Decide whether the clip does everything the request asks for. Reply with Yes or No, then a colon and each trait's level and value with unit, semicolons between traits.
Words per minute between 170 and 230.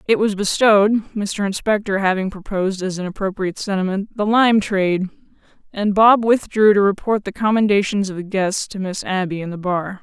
Yes: average, 180 wpm